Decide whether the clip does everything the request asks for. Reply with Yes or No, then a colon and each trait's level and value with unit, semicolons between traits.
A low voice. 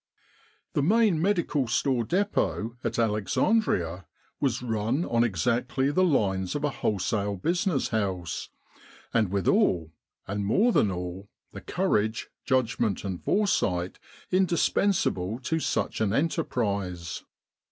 Yes: low, 115 Hz